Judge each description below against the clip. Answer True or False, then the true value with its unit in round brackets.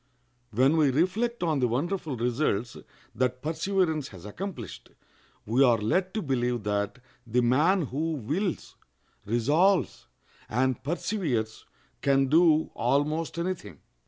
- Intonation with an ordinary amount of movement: False (5.8 semitones)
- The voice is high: False (140 Hz)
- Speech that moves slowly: True (125 wpm)